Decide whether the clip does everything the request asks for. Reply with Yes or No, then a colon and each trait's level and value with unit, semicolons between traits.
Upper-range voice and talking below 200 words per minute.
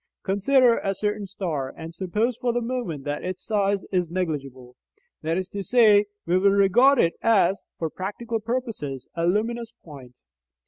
Yes: high, 195 Hz; average, 165 wpm